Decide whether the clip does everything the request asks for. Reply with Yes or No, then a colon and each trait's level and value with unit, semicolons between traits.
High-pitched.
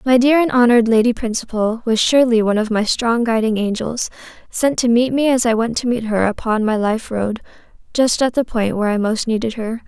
Yes: high, 230 Hz